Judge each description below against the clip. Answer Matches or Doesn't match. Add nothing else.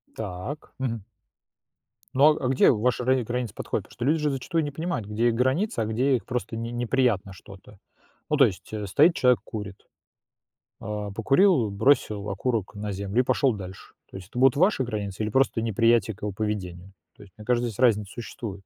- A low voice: Matches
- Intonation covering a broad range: Doesn't match